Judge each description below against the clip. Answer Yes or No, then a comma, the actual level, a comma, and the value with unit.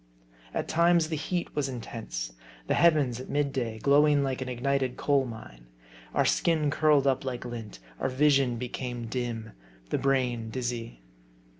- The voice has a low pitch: Yes, low, 130 Hz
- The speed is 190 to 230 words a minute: No, average, 155 wpm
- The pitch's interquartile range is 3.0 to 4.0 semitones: Yes, average, 3.3 semitones